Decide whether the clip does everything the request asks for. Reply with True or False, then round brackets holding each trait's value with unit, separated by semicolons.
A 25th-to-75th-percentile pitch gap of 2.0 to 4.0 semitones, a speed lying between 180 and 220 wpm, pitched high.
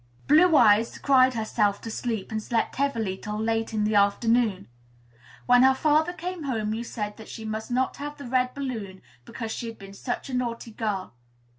True (3.4 semitones; 190 wpm; 230 Hz)